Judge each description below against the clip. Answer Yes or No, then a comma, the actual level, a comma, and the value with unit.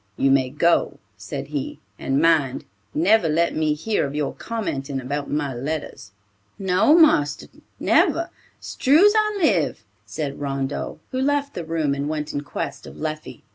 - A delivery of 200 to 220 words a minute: No, average, 155 wpm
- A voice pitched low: No, medium, 150 Hz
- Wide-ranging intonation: Yes, wide, 5.8 semitones